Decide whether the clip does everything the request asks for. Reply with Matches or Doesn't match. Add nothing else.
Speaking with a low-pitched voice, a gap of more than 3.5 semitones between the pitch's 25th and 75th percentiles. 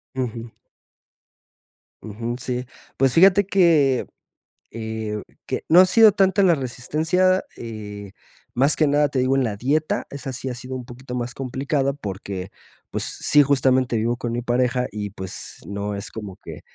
Matches